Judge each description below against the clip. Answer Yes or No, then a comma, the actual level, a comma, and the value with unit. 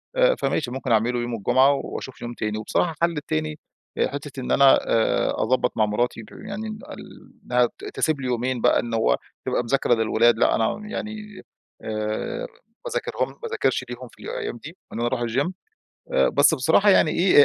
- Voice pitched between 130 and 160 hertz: Yes, low, 135 Hz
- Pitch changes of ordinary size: No, wide, 7.0 semitones